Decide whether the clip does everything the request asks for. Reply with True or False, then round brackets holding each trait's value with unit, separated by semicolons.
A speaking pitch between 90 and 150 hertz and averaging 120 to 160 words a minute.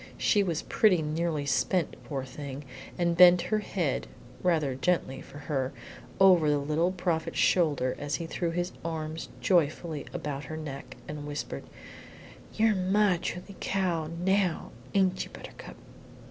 False (165 Hz; 145 wpm)